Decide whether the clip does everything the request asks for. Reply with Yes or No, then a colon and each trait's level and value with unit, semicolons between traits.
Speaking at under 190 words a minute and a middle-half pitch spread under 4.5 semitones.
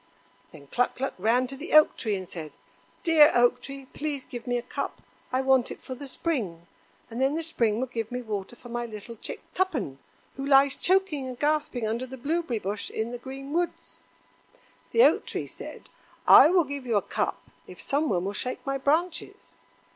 No: average, 200 wpm; average, 4.0 semitones